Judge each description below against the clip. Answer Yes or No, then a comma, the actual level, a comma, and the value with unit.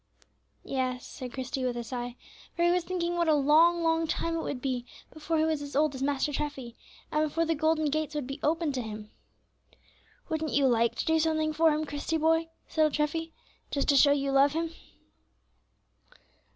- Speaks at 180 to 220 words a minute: Yes, average, 200 wpm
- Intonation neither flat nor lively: Yes, average, 3.1 semitones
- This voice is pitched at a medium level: No, very high, 300 Hz